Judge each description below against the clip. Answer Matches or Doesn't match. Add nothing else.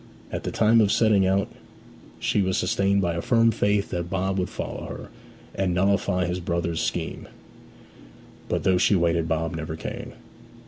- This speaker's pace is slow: Doesn't match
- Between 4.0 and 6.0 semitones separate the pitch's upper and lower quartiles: Doesn't match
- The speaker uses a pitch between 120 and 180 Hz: Doesn't match